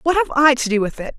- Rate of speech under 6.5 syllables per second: No, 6.9 syllables/s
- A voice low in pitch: No, very high, 270 Hz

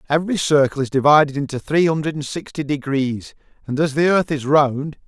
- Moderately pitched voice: Yes, medium, 145 Hz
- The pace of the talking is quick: No, average, 190 wpm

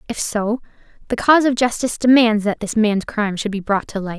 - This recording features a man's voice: No, female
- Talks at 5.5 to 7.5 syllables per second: Yes, 6.0 syllables/s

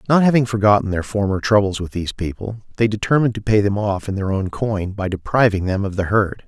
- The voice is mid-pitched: No, low, 105 Hz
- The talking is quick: Yes, fast, 230 wpm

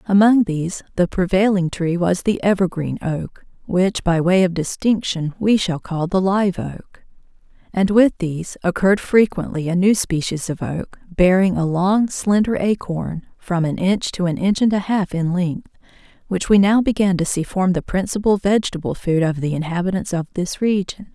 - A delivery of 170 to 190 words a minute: Yes, average, 180 wpm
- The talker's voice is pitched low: No, medium, 185 Hz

